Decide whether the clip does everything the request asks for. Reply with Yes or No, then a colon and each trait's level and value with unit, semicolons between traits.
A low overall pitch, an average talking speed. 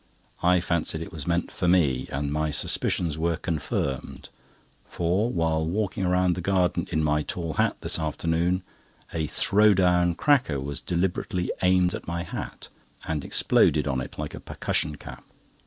Yes: very low, 85 Hz; average, 160 wpm